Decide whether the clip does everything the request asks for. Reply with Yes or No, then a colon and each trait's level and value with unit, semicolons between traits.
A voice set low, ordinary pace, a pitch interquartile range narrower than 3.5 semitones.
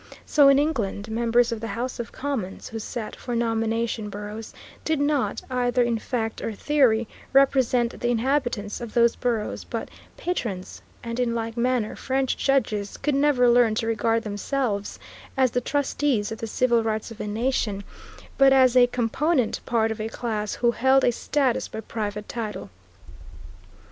No: high, 235 Hz; average, 165 wpm; average, 2.8 semitones